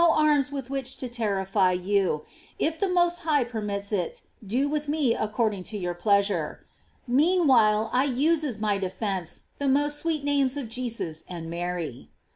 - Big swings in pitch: Yes, wide, 6.5 semitones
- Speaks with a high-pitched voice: Yes, high, 235 Hz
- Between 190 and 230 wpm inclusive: No, average, 160 wpm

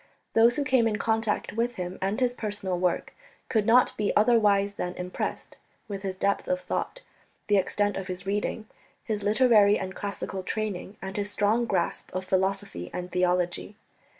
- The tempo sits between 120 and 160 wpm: No, average, 170 wpm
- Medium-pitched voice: No, high, 205 Hz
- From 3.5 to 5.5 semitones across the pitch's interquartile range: No, average, 2.8 semitones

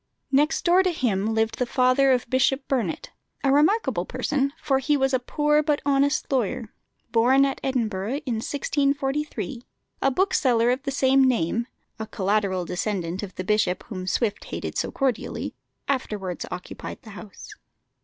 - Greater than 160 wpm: No, average, 155 wpm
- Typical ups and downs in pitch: Yes, average, 4.5 semitones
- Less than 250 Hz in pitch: No, very high, 255 Hz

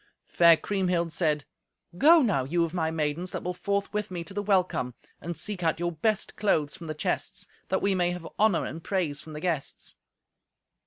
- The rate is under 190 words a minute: No, average, 200 wpm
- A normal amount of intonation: Yes, average, 3.5 semitones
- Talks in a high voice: No, medium, 175 Hz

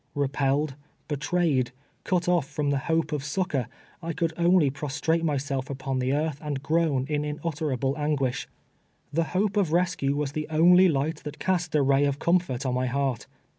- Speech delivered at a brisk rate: No, average, 175 wpm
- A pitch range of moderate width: Yes, average, 3.3 semitones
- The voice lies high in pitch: No, medium, 150 Hz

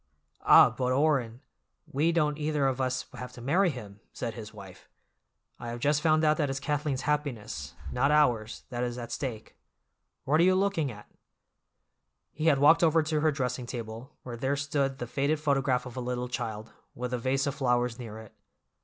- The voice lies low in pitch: Yes, low, 130 Hz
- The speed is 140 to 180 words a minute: No, average, 190 wpm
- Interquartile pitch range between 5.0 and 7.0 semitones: No, average, 3.6 semitones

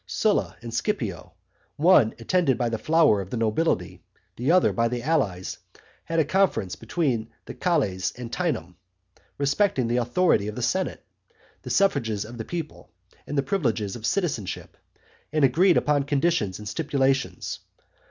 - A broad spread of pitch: Yes, wide, 6.5 semitones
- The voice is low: Yes, low, 130 Hz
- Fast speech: No, average, 150 wpm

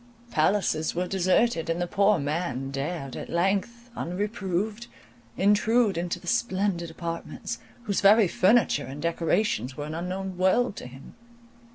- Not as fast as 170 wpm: Yes, average, 140 wpm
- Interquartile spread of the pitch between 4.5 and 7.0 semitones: No, average, 3.8 semitones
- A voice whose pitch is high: No, medium, 180 Hz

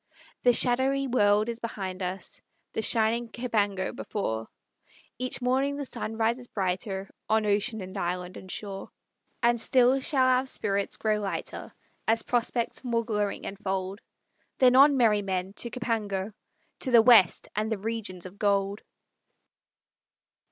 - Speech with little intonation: No, average, 3.7 semitones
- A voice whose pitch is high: Yes, high, 220 Hz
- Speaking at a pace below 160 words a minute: Yes, average, 140 wpm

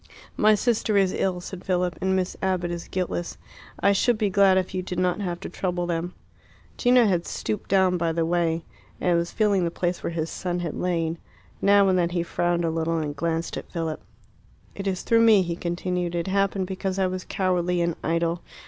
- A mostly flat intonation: Yes, narrow, 1.9 semitones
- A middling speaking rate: No, fast, 210 wpm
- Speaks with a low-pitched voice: No, medium, 180 Hz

